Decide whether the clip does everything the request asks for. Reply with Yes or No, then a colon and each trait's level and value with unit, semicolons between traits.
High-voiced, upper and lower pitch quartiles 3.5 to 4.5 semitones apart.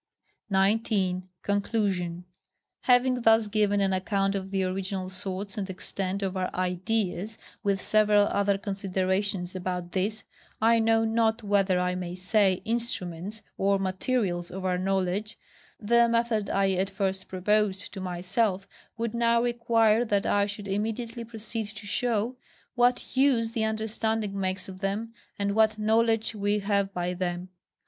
No: high, 200 Hz; average, 2.9 semitones